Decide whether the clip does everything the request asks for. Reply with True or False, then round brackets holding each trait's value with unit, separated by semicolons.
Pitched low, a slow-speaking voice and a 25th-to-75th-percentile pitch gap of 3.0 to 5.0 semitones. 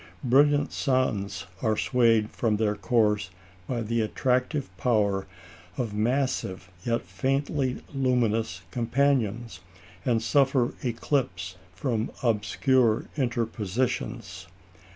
True (115 Hz; 90 wpm; 3.6 semitones)